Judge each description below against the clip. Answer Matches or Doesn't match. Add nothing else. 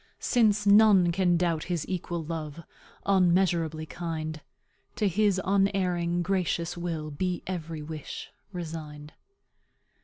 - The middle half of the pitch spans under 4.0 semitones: Matches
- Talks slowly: Matches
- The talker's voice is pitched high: Doesn't match